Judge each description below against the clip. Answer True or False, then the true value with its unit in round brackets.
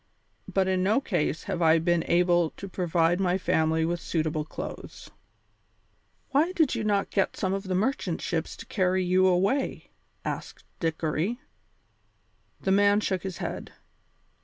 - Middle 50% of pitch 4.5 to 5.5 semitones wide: False (2.9 semitones)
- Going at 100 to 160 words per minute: True (150 wpm)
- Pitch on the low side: False (185 Hz)